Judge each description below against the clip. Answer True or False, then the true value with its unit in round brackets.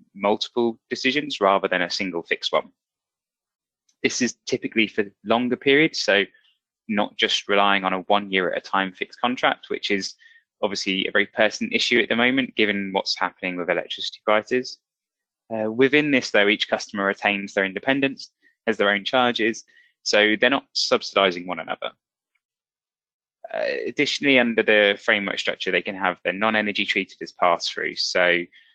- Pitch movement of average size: True (4.2 semitones)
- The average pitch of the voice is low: True (105 Hz)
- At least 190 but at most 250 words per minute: False (165 wpm)